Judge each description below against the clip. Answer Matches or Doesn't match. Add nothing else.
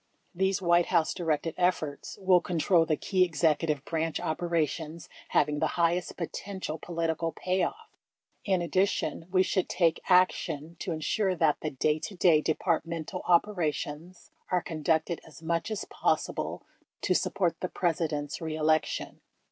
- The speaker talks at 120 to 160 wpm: Matches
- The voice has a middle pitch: Matches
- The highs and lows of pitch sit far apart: Doesn't match